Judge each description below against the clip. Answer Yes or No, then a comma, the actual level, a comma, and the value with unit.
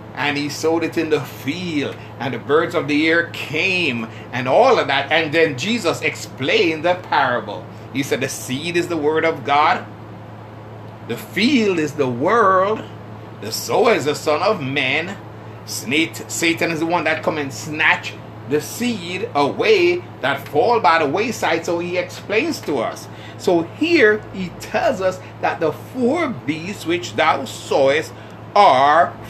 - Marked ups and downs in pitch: Yes, wide, 7.5 semitones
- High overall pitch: No, medium, 150 Hz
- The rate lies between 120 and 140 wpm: No, average, 160 wpm